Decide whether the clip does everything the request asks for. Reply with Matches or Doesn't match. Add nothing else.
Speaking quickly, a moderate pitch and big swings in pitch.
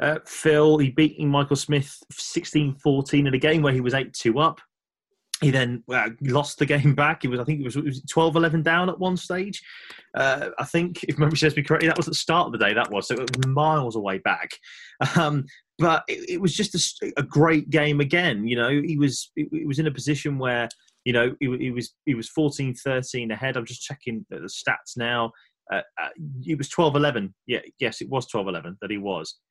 Doesn't match